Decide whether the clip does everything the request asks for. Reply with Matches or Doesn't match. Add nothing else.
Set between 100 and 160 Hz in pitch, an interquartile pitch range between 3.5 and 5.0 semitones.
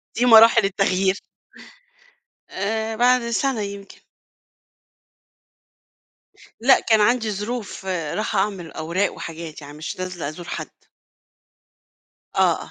Doesn't match